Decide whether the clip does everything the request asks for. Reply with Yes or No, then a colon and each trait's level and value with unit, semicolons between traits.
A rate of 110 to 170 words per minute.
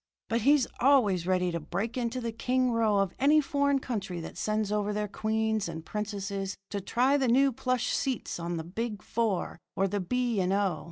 No: average, 200 wpm